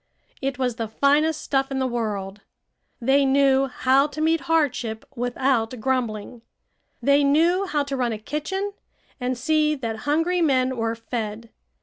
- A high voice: Yes, very high, 265 Hz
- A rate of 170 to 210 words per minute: No, average, 150 wpm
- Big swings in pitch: No, average, 4.1 semitones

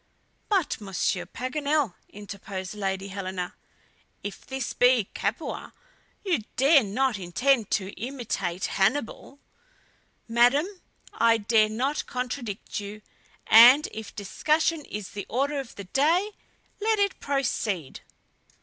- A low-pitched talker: No, high, 235 Hz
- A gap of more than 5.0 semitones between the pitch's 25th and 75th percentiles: Yes, wide, 5.6 semitones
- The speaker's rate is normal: No, slow, 115 wpm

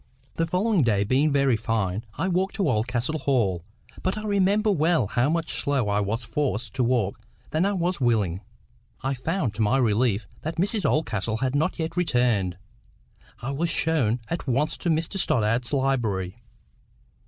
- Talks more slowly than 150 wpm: No, average, 165 wpm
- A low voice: Yes, low, 130 Hz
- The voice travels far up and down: Yes, wide, 6.7 semitones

